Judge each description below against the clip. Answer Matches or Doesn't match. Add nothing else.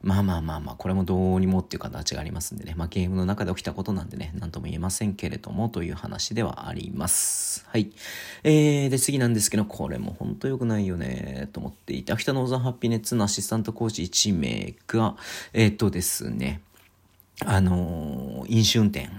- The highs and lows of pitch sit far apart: Doesn't match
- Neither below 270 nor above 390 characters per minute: Doesn't match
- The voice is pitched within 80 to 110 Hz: Matches